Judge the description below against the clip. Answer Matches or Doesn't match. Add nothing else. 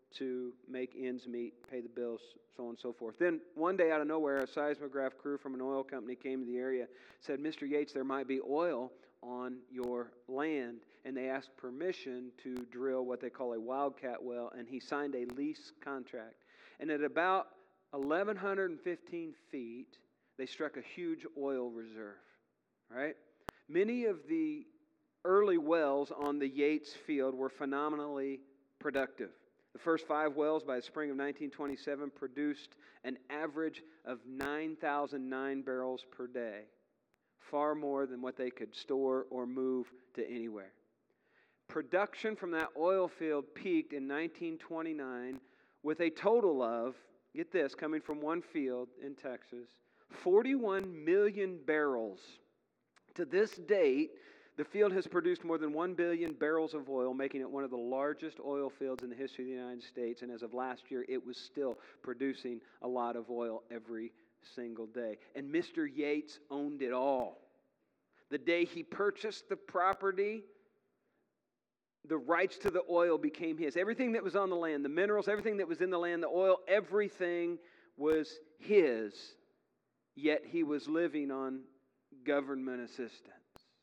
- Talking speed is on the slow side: Doesn't match